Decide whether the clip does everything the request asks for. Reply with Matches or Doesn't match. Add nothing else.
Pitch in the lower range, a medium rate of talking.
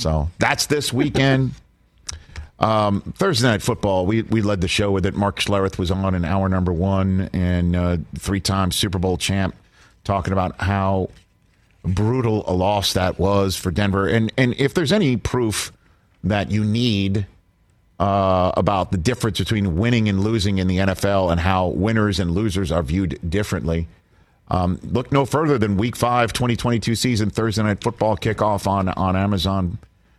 Matches